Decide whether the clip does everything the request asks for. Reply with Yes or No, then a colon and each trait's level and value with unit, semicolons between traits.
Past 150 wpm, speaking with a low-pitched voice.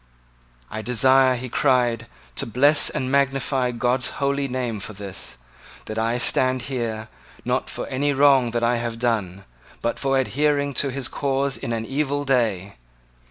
Yes: average, 160 wpm; low, 125 Hz